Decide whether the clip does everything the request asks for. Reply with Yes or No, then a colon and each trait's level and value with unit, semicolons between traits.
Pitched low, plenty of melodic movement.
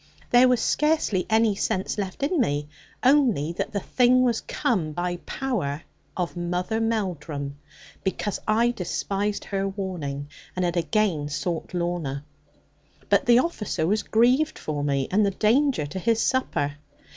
No: high, 195 Hz; wide, 5.9 semitones